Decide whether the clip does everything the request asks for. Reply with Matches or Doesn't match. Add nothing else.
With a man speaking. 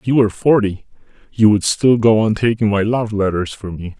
Matches